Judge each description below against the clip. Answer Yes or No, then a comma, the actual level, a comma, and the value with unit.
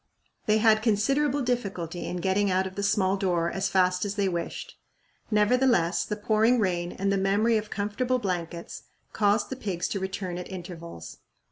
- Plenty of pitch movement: No, average, 3.0 semitones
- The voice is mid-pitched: No, high, 200 Hz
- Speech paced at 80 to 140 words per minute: No, average, 170 wpm